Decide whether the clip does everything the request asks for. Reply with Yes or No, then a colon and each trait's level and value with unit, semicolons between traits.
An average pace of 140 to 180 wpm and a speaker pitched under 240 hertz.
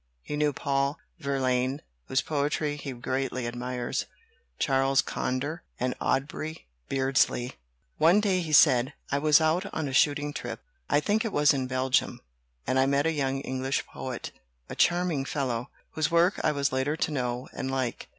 Yes: average, 165 wpm; medium, 140 Hz